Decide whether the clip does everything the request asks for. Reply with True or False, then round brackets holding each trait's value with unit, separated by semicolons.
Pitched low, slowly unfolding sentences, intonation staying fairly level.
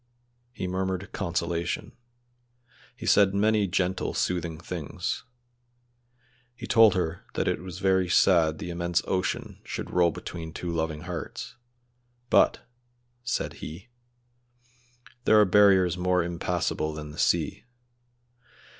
True (90 Hz; 120 wpm; 2.0 semitones)